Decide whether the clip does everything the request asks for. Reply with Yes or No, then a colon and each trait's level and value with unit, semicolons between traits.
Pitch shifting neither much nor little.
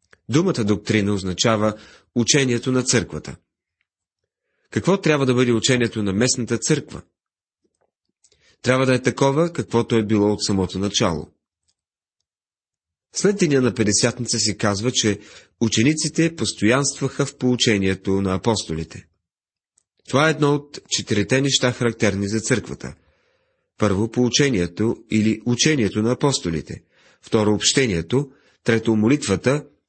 Yes: average, 4.1 semitones